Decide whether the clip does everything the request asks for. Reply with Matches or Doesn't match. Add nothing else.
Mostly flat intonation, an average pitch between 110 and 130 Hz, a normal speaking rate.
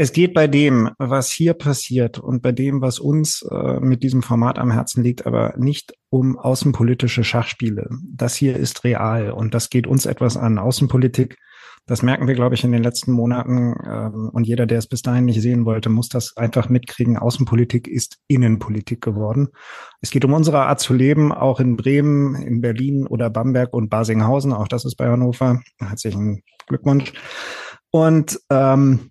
Matches